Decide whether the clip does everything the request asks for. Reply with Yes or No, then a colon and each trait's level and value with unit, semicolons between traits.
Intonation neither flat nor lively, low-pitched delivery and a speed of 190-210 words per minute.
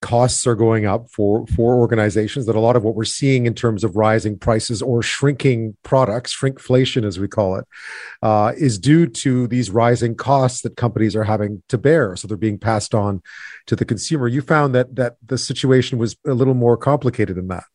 Yes: average, 3.0 semitones; low, 120 Hz; fast, 205 wpm